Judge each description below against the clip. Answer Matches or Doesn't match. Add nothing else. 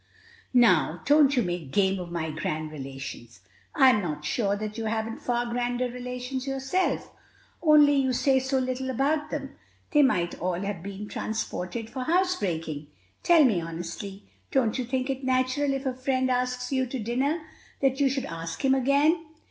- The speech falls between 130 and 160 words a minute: Doesn't match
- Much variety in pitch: Matches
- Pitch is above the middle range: Matches